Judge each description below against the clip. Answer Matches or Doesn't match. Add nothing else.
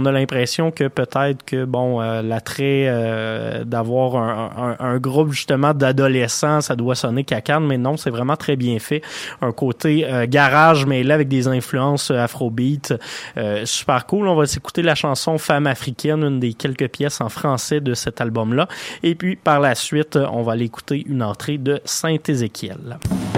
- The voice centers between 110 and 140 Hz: Matches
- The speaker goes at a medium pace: Matches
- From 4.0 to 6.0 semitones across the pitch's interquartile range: Doesn't match